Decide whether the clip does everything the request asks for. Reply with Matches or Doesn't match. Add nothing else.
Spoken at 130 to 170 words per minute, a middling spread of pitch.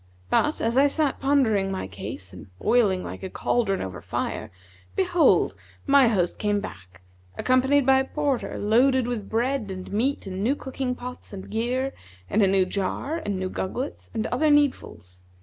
Doesn't match